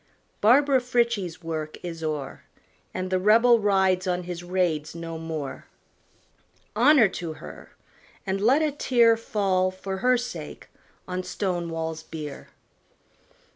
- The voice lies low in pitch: No, medium, 185 Hz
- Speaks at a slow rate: Yes, slow, 125 wpm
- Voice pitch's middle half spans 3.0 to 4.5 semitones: No, wide, 5.6 semitones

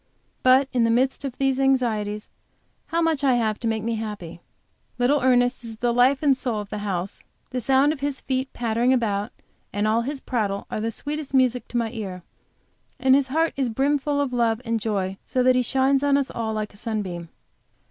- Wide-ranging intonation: No, average, 3.6 semitones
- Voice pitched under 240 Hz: No, high, 245 Hz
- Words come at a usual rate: No, fast, 210 wpm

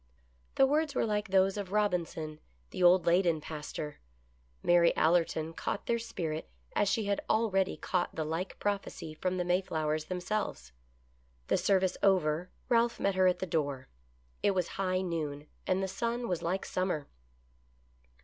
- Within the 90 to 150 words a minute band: No, average, 160 wpm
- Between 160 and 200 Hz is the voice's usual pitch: Yes, medium, 185 Hz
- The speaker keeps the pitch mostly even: No, average, 3.7 semitones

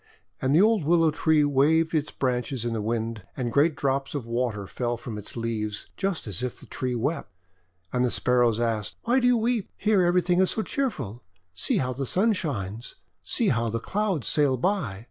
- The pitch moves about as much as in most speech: No, wide, 7.0 semitones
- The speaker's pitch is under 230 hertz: Yes, low, 135 Hz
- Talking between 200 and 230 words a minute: Yes, fast, 205 wpm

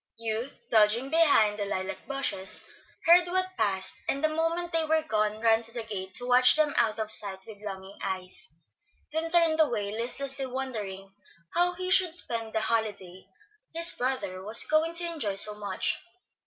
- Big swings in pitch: Yes, wide, 7.2 semitones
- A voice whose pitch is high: Yes, high, 230 Hz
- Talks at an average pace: Yes, average, 170 wpm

